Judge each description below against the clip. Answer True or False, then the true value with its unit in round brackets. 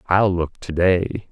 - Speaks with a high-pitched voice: False (90 Hz)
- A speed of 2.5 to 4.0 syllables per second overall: True (3.6 syllables/s)